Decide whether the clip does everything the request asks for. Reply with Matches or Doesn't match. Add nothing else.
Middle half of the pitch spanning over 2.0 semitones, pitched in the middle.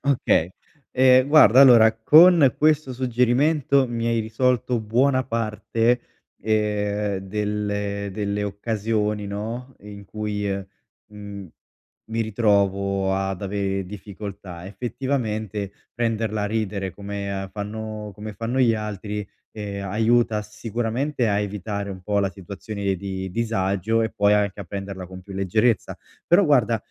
Doesn't match